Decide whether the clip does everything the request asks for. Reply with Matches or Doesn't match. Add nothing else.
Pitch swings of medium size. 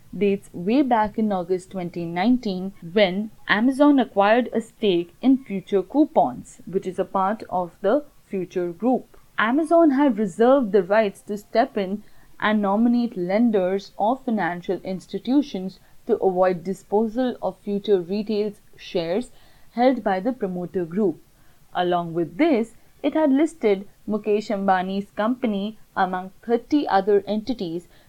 Matches